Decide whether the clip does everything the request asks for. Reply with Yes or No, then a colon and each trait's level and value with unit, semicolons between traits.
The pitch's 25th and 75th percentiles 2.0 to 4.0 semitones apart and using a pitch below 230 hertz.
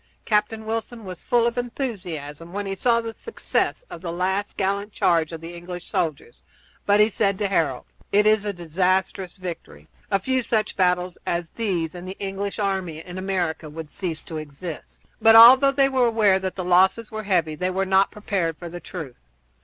Yes: average, 3.6 semitones; high, 190 Hz